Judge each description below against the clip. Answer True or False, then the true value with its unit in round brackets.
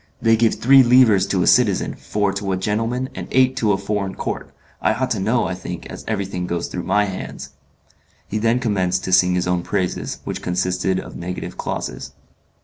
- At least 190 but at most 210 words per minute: True (200 wpm)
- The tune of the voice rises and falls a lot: False (3.6 semitones)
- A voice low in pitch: True (100 Hz)